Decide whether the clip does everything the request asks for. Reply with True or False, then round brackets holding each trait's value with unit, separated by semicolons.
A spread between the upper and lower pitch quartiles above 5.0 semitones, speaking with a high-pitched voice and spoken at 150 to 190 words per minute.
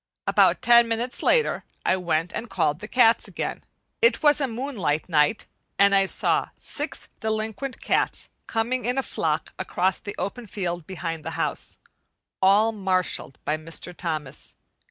True (5.5 semitones; 200 Hz; 155 wpm)